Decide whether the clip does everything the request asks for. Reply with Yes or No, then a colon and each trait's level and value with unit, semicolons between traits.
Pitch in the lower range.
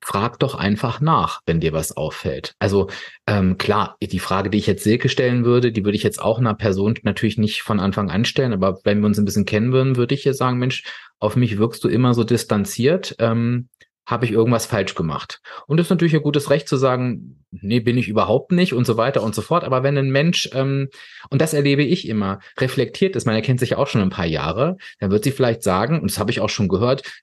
Yes: low, 115 Hz